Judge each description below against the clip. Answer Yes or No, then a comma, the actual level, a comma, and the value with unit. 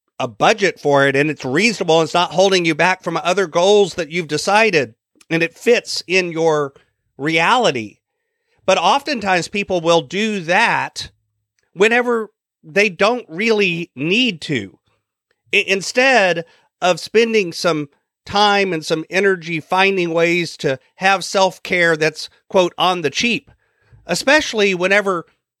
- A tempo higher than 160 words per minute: No, slow, 135 wpm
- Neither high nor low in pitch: Yes, medium, 180 Hz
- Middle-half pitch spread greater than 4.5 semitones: No, average, 3.9 semitones